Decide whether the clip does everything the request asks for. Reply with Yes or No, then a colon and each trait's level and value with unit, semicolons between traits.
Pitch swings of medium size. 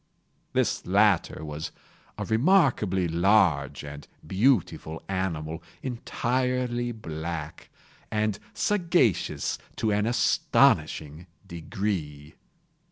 No: wide, 6.8 semitones